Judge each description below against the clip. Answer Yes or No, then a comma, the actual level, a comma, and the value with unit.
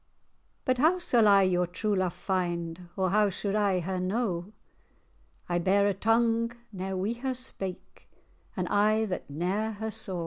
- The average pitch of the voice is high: Yes, high, 195 Hz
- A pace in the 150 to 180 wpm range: Yes, average, 165 wpm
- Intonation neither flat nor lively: Yes, average, 3.3 semitones